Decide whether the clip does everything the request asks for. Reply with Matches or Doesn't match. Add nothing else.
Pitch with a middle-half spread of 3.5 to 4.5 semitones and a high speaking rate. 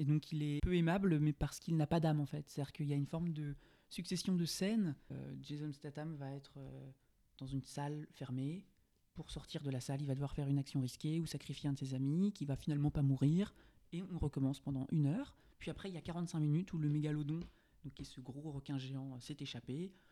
Doesn't match